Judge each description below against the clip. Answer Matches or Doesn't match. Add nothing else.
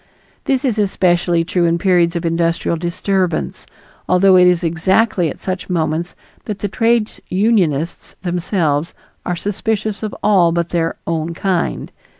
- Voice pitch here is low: Doesn't match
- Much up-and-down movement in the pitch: Doesn't match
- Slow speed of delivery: Doesn't match